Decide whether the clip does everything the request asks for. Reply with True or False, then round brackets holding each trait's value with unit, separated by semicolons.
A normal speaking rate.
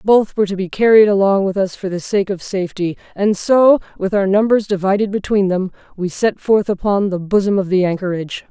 False (210 wpm)